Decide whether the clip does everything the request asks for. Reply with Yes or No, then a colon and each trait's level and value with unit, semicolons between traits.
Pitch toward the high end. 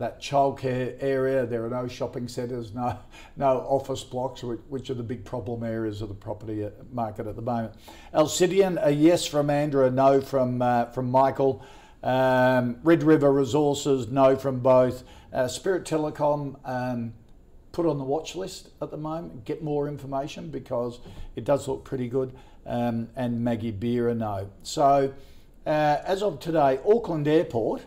No: low, 130 Hz